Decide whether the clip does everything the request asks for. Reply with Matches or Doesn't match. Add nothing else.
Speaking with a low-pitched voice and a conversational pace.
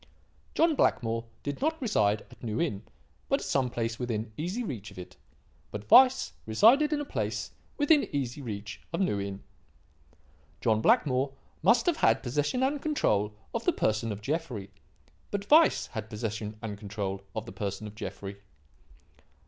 Matches